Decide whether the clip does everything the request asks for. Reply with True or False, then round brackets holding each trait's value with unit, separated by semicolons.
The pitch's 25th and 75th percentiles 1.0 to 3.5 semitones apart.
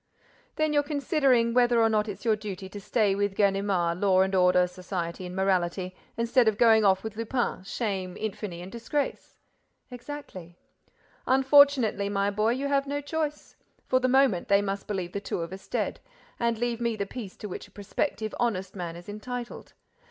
False (4.4 semitones)